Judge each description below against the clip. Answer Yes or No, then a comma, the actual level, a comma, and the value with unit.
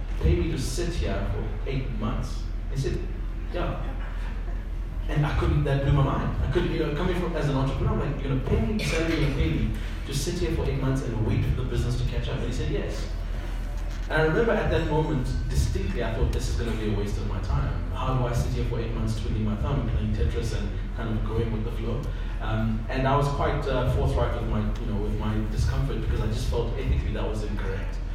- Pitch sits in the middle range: No, low, 110 Hz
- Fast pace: Yes, fast, 250 wpm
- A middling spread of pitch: Yes, average, 4.4 semitones